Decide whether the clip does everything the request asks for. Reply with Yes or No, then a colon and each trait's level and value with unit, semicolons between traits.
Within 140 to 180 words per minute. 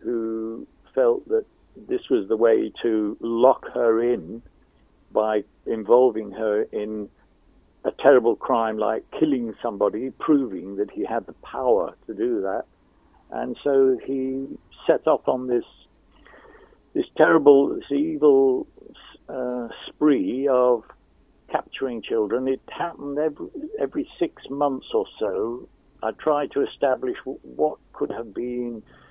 No: average, 130 wpm